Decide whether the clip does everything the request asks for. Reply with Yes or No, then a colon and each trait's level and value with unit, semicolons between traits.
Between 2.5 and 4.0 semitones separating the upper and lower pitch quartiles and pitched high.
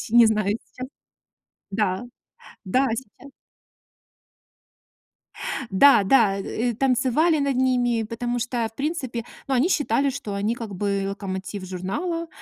No: average, 4.4 semitones; high, 235 Hz